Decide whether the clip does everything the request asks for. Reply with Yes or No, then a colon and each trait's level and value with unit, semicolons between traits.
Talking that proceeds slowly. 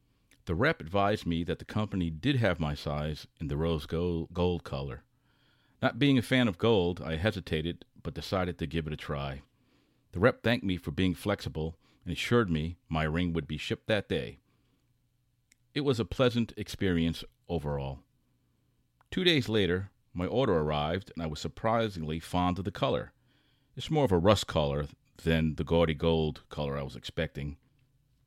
No: average, 175 wpm